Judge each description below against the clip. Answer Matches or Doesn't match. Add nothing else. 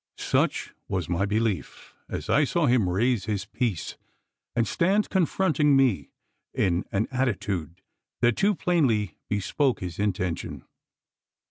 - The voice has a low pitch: Matches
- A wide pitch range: Matches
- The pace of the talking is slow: Matches